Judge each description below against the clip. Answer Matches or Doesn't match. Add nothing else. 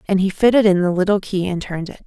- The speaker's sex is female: Matches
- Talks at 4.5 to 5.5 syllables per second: Doesn't match